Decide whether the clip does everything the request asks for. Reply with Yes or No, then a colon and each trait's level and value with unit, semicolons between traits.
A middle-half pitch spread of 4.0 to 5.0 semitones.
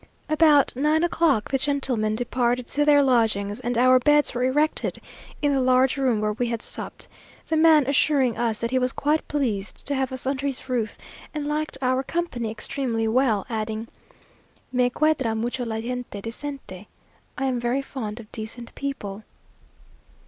No: average, 3.6 semitones